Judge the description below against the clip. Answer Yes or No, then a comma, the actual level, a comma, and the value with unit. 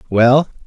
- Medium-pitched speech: No, low, 130 Hz